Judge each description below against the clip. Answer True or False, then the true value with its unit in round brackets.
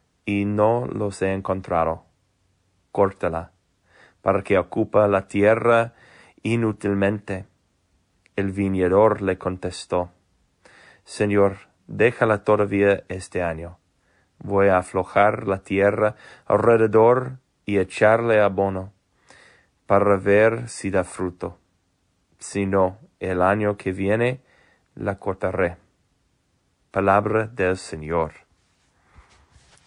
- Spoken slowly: True (90 wpm)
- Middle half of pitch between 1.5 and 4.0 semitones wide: True (2.4 semitones)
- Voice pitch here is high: False (95 Hz)